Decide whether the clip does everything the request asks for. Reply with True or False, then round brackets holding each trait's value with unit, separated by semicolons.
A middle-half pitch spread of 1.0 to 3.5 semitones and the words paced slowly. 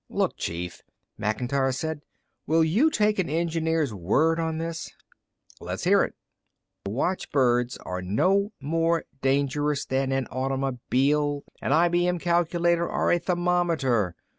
False (4.5 semitones; 125 wpm)